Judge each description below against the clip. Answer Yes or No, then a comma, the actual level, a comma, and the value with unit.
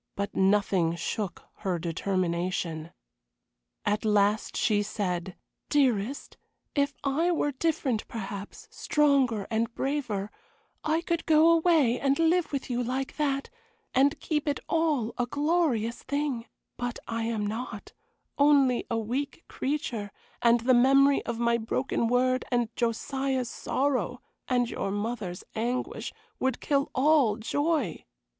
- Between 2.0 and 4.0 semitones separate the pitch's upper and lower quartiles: No, average, 5.0 semitones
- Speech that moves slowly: Yes, slow, 130 wpm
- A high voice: Yes, high, 245 Hz